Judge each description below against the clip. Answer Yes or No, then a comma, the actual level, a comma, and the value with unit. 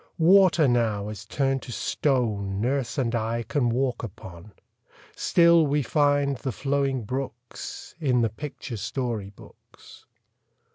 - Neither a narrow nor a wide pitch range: Yes, average, 4.0 semitones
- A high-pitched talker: No, low, 125 Hz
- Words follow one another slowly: Yes, slow, 130 wpm